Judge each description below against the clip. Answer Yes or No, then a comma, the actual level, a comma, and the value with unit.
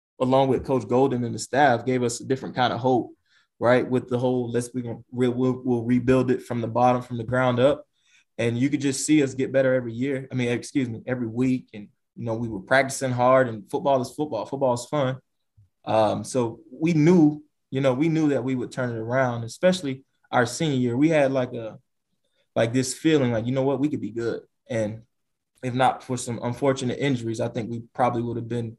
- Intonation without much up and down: Yes, narrow, 2.0 semitones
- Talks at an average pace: No, fast, 225 wpm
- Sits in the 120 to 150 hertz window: Yes, low, 125 Hz